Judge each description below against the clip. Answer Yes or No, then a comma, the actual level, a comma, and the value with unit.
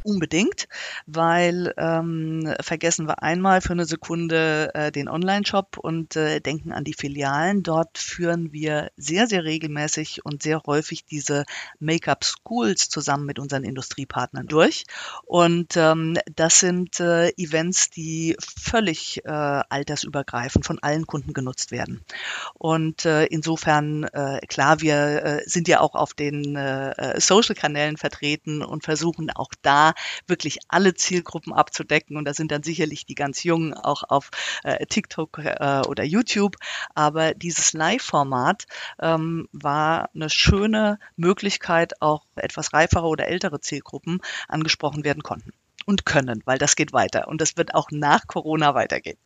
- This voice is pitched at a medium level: Yes, medium, 160 Hz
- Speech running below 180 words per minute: Yes, average, 145 wpm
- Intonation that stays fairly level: Yes, narrow, 2.3 semitones